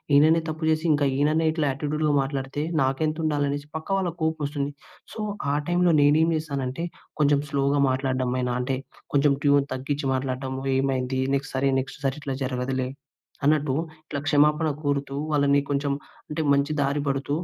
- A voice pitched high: No, medium, 140 Hz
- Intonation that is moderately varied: No, narrow, 2.0 semitones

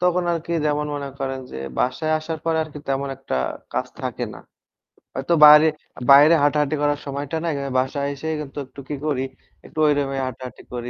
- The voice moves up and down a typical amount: No, narrow, 2.3 semitones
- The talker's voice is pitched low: No, medium, 145 Hz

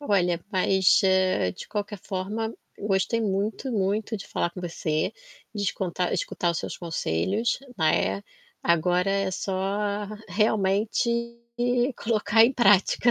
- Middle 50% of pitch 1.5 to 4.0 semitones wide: Yes, average, 2.9 semitones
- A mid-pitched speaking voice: No, high, 195 Hz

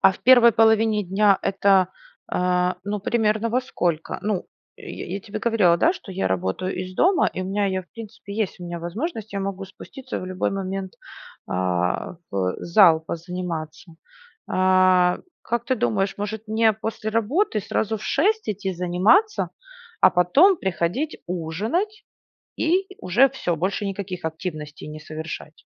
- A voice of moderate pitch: No, high, 195 Hz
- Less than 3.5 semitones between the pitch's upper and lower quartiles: No, average, 3.8 semitones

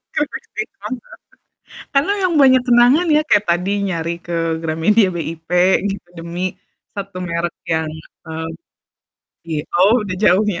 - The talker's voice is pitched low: No, medium, 185 Hz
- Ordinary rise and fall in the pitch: No, wide, 6.2 semitones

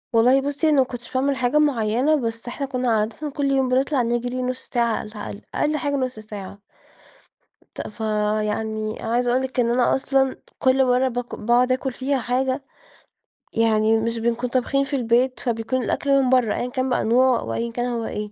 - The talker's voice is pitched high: Yes, high, 245 Hz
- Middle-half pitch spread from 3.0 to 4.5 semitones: No, narrow, 2.5 semitones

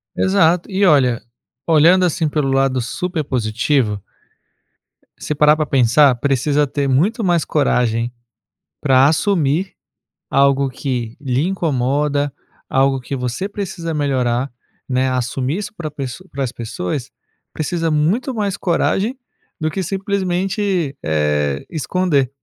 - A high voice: No, medium, 145 Hz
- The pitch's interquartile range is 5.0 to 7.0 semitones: Yes, average, 5.3 semitones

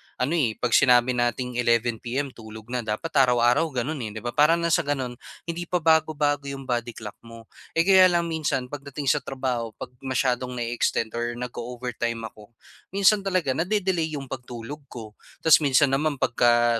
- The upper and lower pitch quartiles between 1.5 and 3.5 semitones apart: No, average, 4.3 semitones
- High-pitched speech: No, low, 130 Hz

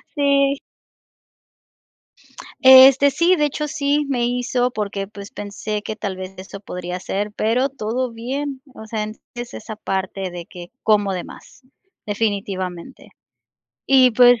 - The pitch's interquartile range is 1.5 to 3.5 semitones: No, average, 4.9 semitones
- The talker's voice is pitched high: Yes, high, 225 Hz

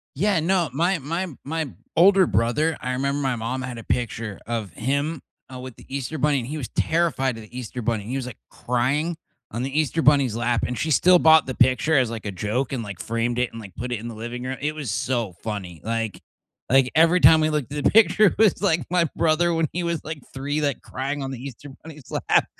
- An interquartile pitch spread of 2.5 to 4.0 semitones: No, average, 4.9 semitones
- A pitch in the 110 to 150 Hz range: Yes, low, 135 Hz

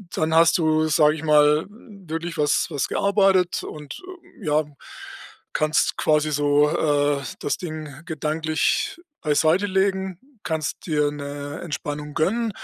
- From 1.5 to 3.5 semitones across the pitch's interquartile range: Yes, average, 2.7 semitones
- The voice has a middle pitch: Yes, medium, 155 Hz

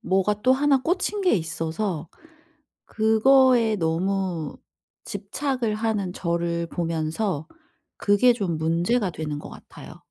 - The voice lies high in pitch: Yes, high, 195 Hz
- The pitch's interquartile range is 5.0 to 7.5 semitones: Yes, wide, 5.6 semitones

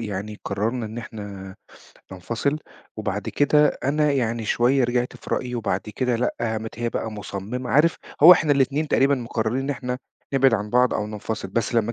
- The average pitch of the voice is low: Yes, low, 120 Hz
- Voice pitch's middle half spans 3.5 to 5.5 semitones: Yes, average, 3.8 semitones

